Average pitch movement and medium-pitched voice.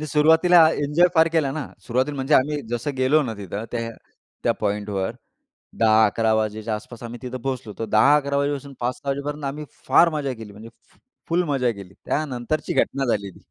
No: average, 4.9 semitones; low, 130 Hz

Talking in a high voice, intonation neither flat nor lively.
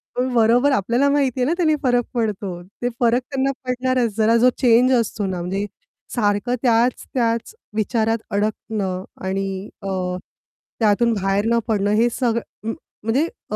Yes: high, 230 Hz; average, 3.3 semitones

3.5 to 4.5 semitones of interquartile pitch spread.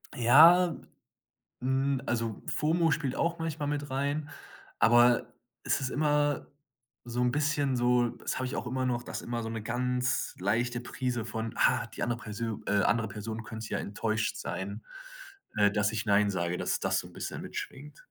Yes: average, 3.9 semitones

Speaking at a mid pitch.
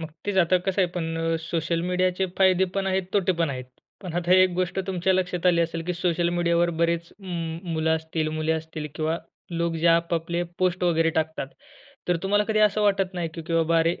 Yes: medium, 170 Hz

